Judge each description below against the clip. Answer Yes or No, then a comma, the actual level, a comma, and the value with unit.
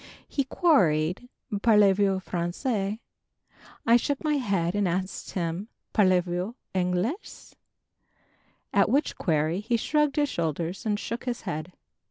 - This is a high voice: Yes, high, 195 Hz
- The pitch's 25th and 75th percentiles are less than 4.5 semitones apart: No, average, 5.3 semitones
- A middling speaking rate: No, slow, 130 wpm